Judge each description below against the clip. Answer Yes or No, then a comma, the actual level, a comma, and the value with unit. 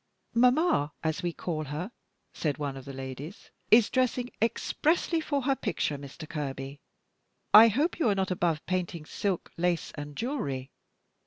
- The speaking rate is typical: Yes, average, 155 wpm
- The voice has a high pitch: No, medium, 175 Hz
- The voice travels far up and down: Yes, wide, 8.5 semitones